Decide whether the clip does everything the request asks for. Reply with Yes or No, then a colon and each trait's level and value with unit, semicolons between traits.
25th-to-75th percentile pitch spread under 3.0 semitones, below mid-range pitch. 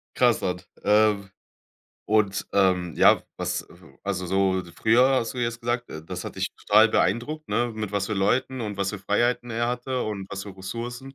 No: average, 3.7 semitones; low, 110 Hz